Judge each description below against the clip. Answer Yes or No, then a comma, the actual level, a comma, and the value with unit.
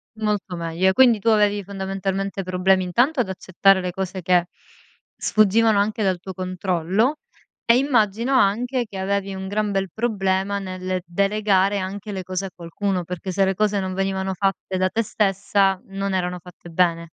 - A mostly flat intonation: Yes, narrow, 1.9 semitones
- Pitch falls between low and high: No, high, 195 Hz